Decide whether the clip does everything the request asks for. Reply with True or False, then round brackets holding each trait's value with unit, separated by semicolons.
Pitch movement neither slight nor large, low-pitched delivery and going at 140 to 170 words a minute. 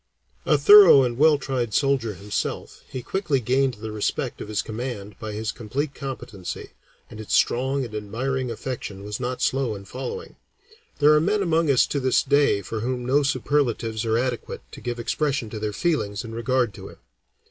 False (4.2 semitones; 125 Hz; 185 wpm)